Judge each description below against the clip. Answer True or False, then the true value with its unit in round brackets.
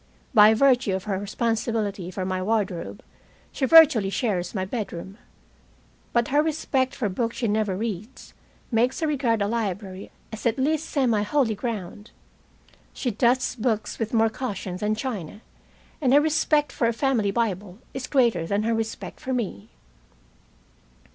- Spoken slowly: False (155 wpm)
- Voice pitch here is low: False (225 Hz)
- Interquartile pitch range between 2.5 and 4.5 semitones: True (4.1 semitones)